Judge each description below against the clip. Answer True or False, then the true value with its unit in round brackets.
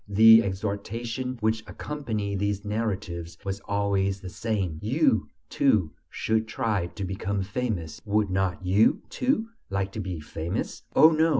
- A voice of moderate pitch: False (100 Hz)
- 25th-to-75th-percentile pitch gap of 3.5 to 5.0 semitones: False (2.8 semitones)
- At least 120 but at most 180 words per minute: True (140 wpm)